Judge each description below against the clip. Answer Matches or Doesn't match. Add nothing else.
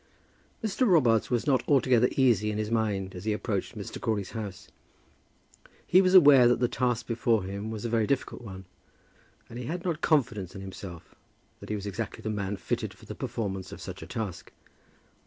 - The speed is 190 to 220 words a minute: Matches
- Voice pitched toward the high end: Doesn't match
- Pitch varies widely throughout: Doesn't match